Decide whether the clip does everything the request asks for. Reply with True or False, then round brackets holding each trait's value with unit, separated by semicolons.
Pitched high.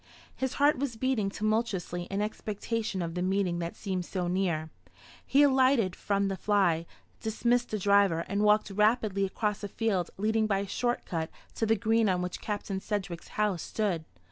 True (205 Hz)